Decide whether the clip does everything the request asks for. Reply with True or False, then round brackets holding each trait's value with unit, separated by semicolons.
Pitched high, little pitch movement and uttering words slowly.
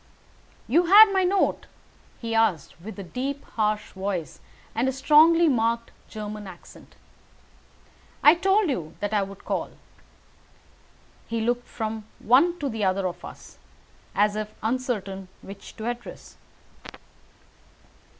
False (225 Hz; 5.3 semitones; 130 wpm)